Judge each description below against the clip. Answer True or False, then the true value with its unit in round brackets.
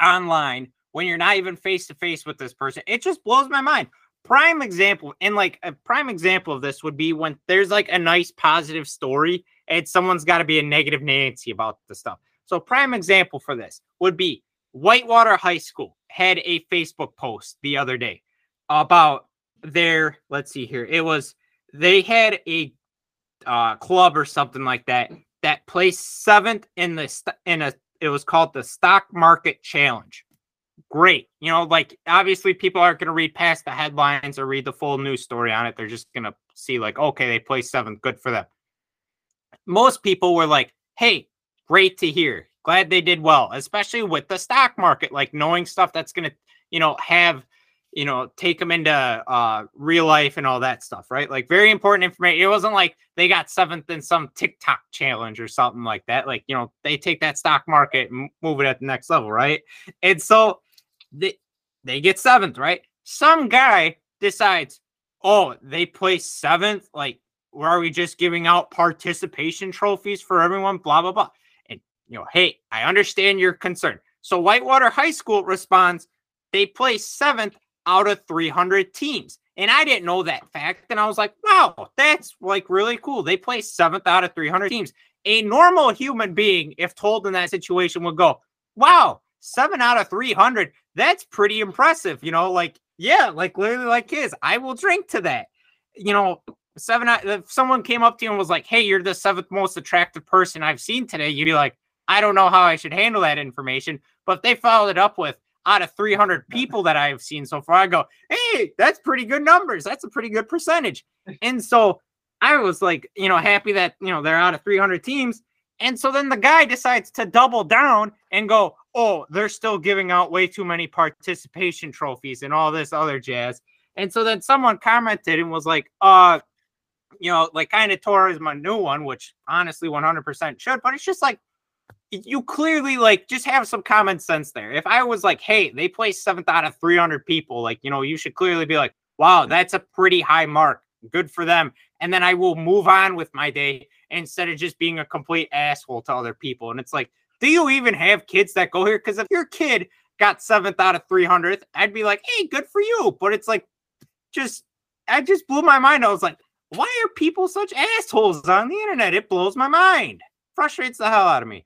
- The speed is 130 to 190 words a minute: False (205 wpm)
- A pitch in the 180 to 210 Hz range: True (185 Hz)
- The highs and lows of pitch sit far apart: True (6.1 semitones)